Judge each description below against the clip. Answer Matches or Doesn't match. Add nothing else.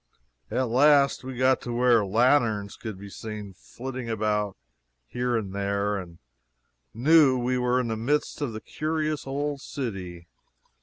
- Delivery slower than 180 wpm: Matches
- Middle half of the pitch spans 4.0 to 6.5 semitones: Matches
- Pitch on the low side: Matches